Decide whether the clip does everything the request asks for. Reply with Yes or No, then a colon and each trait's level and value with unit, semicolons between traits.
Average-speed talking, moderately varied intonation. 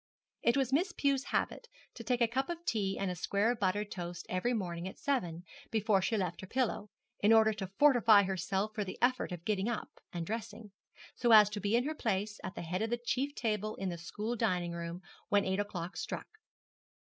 No: fast, 215 wpm; average, 4.0 semitones